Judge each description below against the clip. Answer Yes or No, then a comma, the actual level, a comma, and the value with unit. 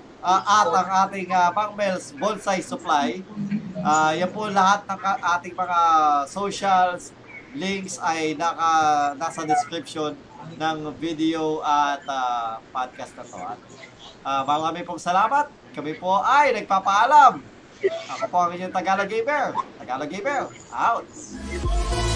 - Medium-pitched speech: Yes, medium, 180 Hz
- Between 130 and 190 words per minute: No, average, 120 wpm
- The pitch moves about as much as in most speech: Yes, average, 4.1 semitones